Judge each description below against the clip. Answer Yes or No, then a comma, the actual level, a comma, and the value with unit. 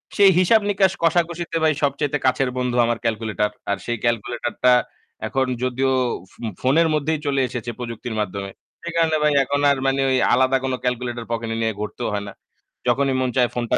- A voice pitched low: Yes, low, 130 Hz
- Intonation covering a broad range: No, average, 4.1 semitones